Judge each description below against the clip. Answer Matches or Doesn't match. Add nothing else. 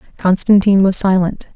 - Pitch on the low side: Doesn't match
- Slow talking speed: Matches